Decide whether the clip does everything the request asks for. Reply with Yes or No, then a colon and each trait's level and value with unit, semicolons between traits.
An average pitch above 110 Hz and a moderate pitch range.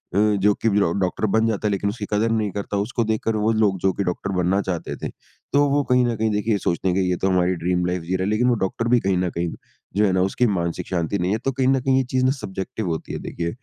No: low, 100 Hz; average, 3.5 semitones